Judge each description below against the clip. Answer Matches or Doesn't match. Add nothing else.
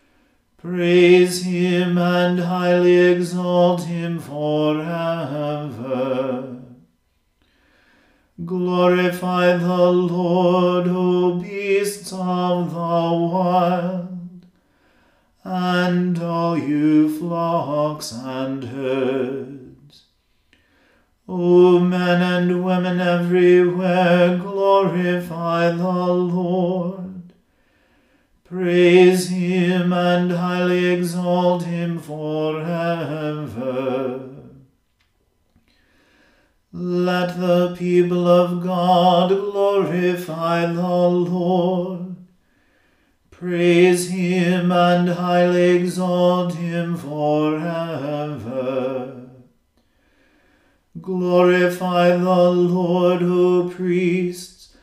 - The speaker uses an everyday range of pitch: Doesn't match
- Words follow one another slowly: Matches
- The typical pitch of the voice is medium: Matches